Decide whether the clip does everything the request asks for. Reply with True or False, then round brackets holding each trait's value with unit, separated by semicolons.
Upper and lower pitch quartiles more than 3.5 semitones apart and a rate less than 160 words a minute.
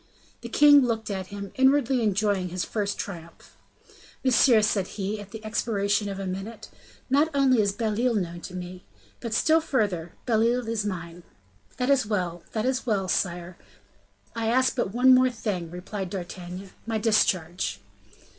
False (4.4 semitones; 165 wpm)